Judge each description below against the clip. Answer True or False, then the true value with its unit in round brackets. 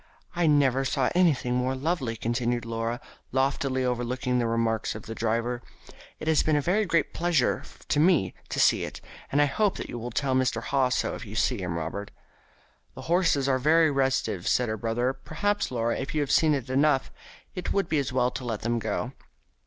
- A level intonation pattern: False (4.0 semitones)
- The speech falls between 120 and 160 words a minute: False (200 wpm)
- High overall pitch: False (130 Hz)